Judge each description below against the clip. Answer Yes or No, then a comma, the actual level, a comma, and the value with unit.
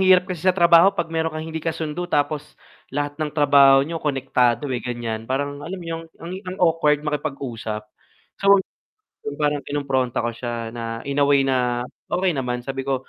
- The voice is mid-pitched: Yes, medium, 145 Hz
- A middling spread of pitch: Yes, average, 4.3 semitones